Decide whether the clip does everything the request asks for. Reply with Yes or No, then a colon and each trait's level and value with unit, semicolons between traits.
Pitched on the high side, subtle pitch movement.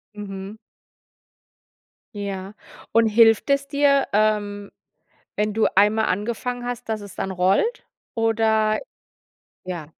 Yes: high, 215 Hz; narrow, 2.2 semitones